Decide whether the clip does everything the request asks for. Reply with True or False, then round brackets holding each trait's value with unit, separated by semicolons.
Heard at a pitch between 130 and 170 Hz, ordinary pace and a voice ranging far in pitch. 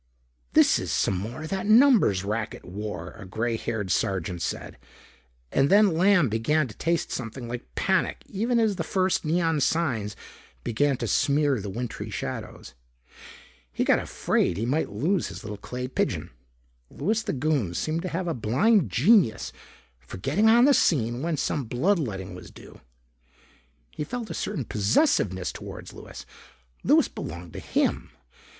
True (135 Hz; 160 wpm; 8.7 semitones)